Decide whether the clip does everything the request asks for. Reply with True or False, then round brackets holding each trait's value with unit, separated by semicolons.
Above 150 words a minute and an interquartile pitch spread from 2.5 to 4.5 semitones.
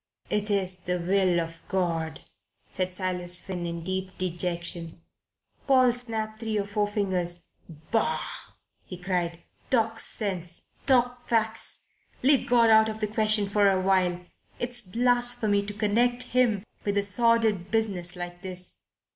False (140 wpm; 3.9 semitones)